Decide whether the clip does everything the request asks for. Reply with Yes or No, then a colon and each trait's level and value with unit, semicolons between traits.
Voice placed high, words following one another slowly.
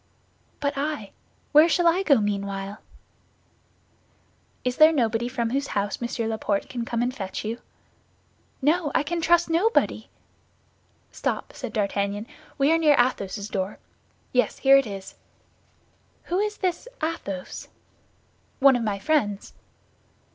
Yes: very high, 250 Hz; slow, 130 wpm